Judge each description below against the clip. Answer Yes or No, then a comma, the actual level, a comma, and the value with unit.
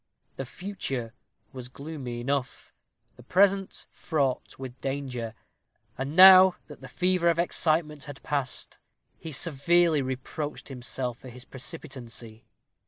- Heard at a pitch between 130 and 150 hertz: Yes, medium, 140 Hz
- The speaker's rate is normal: No, slow, 120 wpm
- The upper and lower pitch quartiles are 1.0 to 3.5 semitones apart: No, average, 4.6 semitones